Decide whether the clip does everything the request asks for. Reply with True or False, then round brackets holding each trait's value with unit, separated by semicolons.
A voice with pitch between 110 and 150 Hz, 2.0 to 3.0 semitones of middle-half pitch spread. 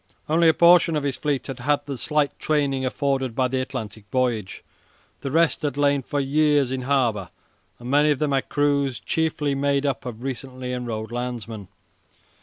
True (135 Hz; 2.6 semitones)